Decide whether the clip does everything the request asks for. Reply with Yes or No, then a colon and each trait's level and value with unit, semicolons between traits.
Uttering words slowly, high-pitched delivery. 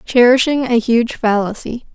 Yes: slow, 125 wpm; high, 235 Hz